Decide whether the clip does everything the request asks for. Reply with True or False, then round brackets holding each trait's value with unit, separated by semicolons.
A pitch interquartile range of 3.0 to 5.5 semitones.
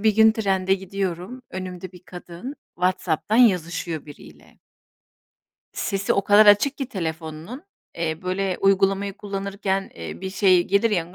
False (2.4 semitones)